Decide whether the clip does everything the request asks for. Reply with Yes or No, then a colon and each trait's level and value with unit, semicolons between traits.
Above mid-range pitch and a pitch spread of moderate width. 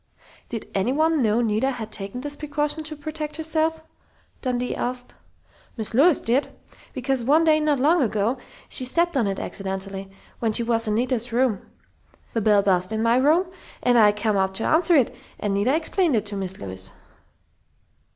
No: high, 245 Hz; wide, 6.0 semitones